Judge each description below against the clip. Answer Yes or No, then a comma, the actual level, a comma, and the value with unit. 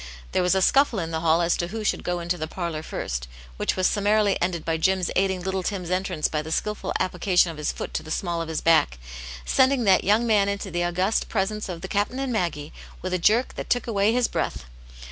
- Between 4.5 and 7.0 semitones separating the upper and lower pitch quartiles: No, average, 3.5 semitones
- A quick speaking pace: Yes, fast, 240 wpm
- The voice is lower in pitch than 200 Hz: Yes, medium, 185 Hz